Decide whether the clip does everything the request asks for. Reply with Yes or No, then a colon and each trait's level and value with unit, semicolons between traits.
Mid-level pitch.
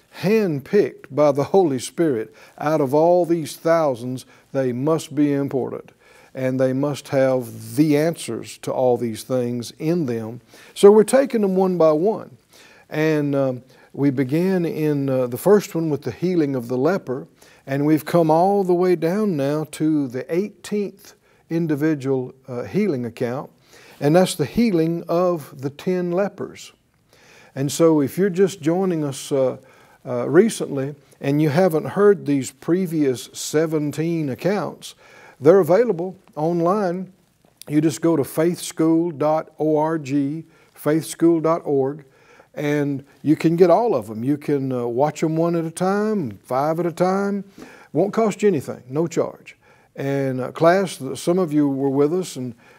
Yes: medium, 155 Hz